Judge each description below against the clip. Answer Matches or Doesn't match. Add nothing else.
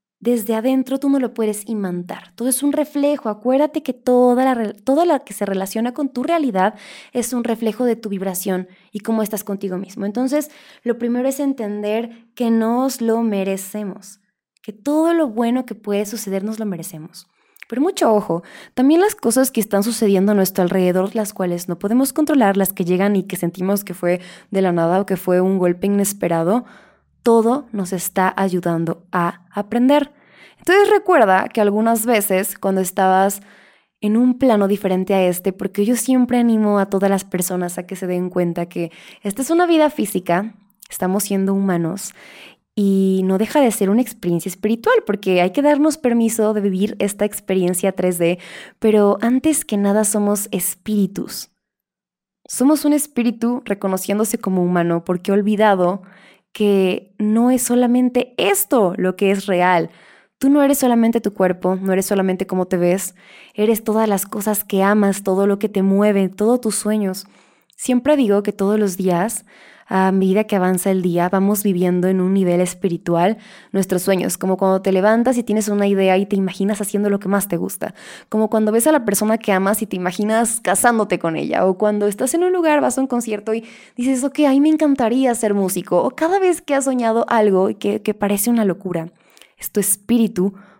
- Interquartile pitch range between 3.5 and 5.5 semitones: Matches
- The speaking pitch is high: Matches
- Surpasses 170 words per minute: Matches